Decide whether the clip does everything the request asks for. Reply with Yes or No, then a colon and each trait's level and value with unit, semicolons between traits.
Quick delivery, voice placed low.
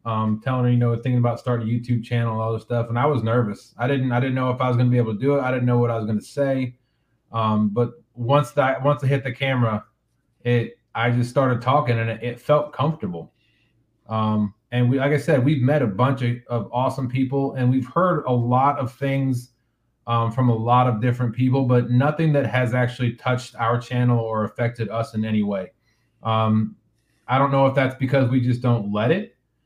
Yes: fast, 235 wpm; low, 125 Hz